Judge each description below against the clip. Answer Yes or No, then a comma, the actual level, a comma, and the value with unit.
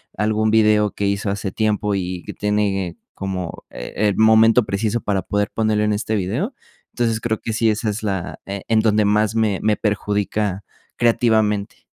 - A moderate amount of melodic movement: No, narrow, 1.6 semitones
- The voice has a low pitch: Yes, low, 105 Hz